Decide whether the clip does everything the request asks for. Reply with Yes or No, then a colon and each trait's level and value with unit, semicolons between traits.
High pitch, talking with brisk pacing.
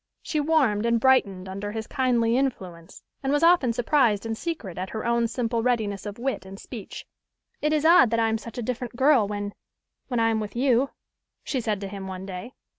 Yes: high, 230 Hz; fast, 210 wpm